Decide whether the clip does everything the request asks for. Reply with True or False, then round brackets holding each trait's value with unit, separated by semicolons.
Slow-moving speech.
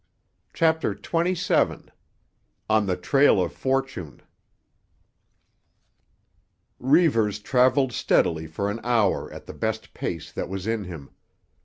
True (105 wpm)